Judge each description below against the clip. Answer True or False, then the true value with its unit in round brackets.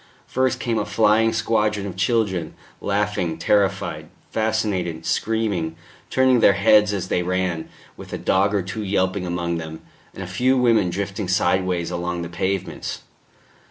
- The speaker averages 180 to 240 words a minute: False (150 wpm)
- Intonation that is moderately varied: True (3.3 semitones)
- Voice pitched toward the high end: False (95 Hz)